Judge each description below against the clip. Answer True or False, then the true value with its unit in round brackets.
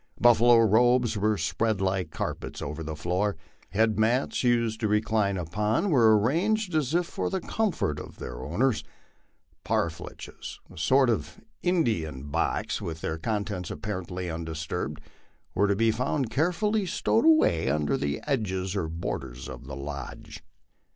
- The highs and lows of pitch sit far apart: True (7.1 semitones)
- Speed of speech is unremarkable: True (150 wpm)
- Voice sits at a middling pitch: False (105 Hz)